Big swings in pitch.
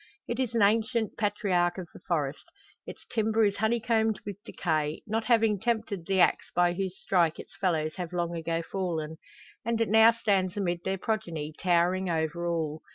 No: average, 4.4 semitones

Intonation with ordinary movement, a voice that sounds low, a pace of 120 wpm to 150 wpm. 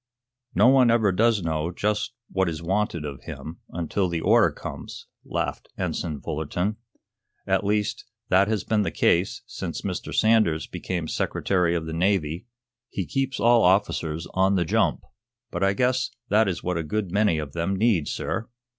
No: average, 4.2 semitones; very low, 95 Hz; average, 170 wpm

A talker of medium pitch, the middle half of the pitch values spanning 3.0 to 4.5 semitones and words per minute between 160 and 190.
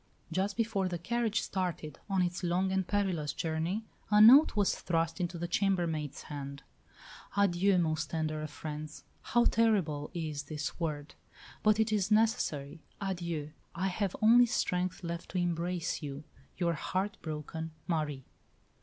No: medium, 175 Hz; average, 4.1 semitones; average, 145 wpm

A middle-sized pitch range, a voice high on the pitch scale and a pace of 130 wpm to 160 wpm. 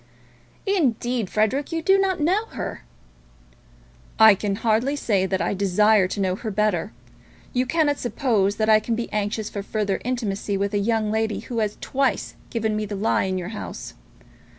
No: average, 3.7 semitones; high, 215 Hz; average, 175 wpm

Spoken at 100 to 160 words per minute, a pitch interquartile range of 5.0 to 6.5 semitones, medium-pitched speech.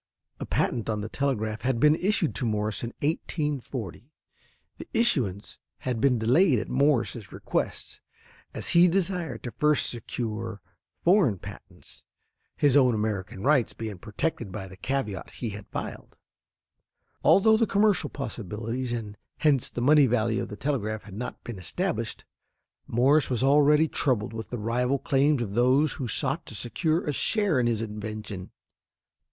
No: average, 155 wpm; wide, 5.4 semitones; low, 125 Hz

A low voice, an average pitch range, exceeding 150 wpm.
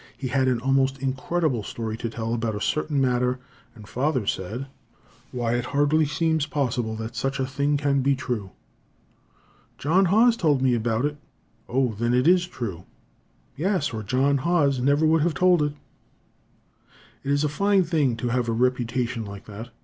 Yes: low, 130 Hz; average, 3.8 semitones; average, 175 wpm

